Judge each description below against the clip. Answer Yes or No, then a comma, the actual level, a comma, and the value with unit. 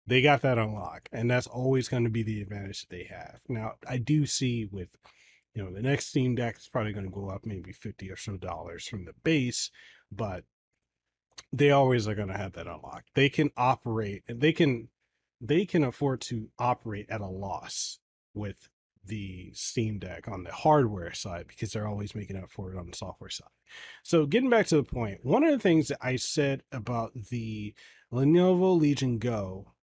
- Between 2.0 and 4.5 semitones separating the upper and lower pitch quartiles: No, average, 5.1 semitones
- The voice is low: Yes, low, 115 Hz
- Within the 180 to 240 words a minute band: Yes, average, 195 wpm